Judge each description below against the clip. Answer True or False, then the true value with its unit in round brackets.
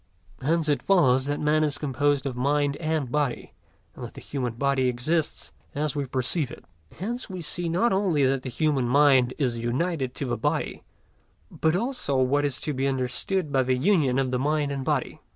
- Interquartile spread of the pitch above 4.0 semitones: False (3.2 semitones)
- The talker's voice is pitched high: False (140 Hz)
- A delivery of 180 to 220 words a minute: True (195 wpm)